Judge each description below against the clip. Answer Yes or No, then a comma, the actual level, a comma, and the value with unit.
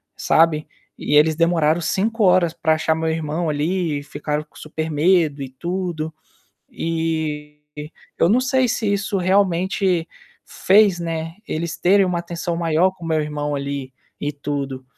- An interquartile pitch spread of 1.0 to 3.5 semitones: Yes, average, 3.1 semitones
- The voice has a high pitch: No, medium, 165 Hz